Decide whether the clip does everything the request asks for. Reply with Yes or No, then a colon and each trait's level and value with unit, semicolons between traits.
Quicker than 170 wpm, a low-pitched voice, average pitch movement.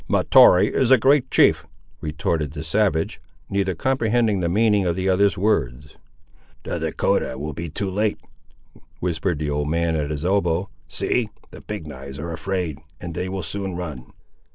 No: average, 165 wpm; very low, 90 Hz; average, 4.5 semitones